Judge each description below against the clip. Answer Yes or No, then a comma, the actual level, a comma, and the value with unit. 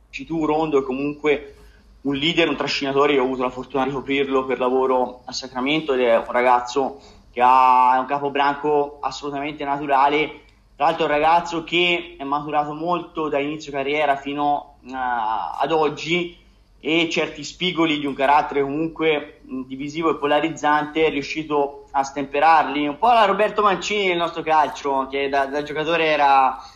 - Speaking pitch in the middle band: Yes, medium, 145 Hz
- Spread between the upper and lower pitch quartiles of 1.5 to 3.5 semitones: Yes, narrow, 2.5 semitones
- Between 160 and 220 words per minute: Yes, average, 165 wpm